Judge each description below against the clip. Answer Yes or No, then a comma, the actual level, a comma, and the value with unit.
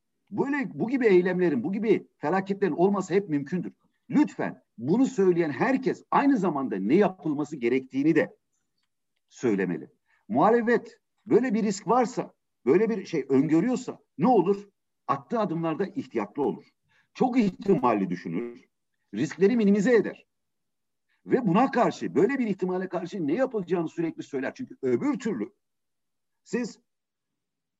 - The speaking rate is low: No, average, 125 wpm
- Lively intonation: Yes, wide, 5.9 semitones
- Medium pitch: No, high, 200 Hz